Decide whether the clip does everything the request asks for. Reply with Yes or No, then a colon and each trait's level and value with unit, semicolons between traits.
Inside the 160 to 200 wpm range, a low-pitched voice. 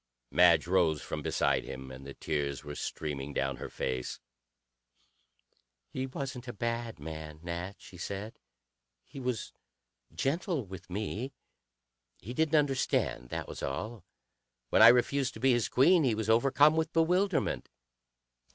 No: average, 140 wpm; low, 110 Hz